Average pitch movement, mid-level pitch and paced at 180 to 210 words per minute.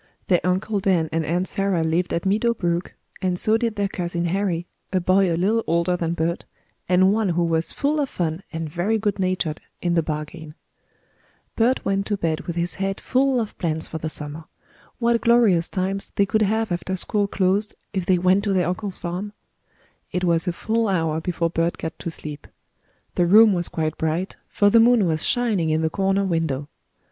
Yes: average, 3.5 semitones; medium, 180 Hz; average, 200 wpm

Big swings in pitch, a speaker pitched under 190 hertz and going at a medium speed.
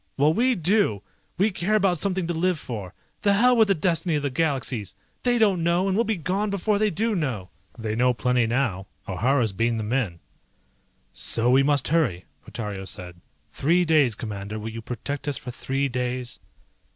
Yes: wide, 8.2 semitones; medium, 140 Hz; average, 190 wpm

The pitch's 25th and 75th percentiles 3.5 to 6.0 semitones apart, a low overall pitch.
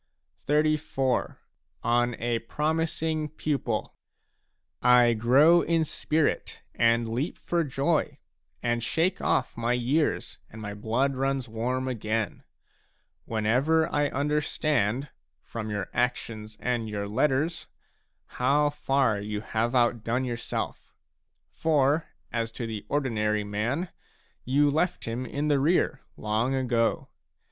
Yes: average, 4.5 semitones; low, 125 Hz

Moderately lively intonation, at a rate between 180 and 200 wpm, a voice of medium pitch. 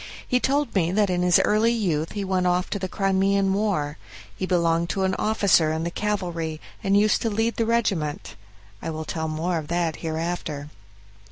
Yes: average, 3.9 semitones; average, 185 wpm; medium, 180 Hz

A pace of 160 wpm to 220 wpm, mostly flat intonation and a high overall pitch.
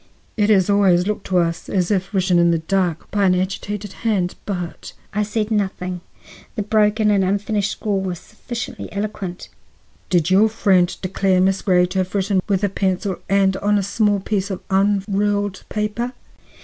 Yes: average, 175 wpm; narrow, 2.0 semitones; high, 195 Hz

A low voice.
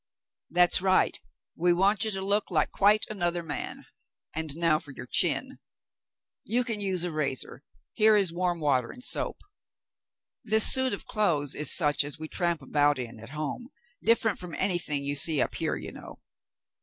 No: medium, 175 Hz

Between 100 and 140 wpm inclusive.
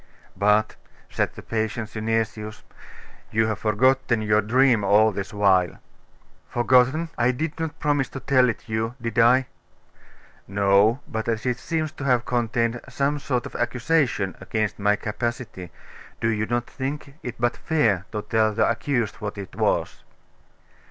No: average, 150 wpm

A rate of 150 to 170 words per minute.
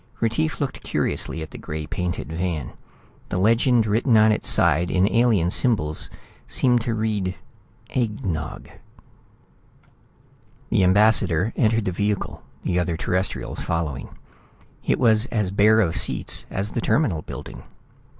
No: slow, 135 wpm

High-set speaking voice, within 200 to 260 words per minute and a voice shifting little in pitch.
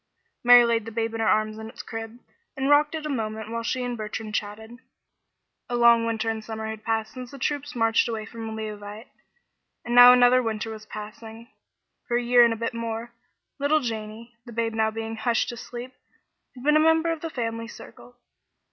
Yes: high, 230 Hz; fast, 205 wpm; narrow, 1.8 semitones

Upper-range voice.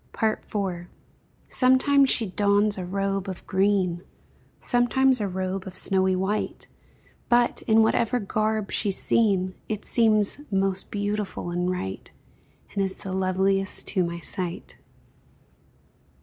Yes: high, 195 Hz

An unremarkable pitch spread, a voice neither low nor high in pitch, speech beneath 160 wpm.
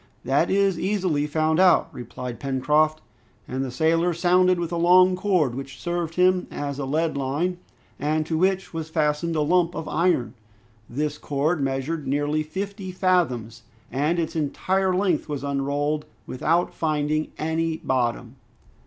Yes: average, 3.8 semitones; medium, 155 Hz; average, 150 wpm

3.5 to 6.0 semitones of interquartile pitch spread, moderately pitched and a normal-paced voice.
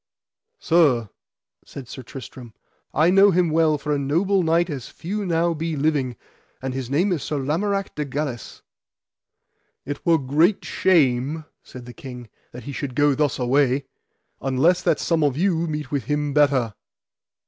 Yes: average, 4.0 semitones; medium, 145 Hz; average, 160 wpm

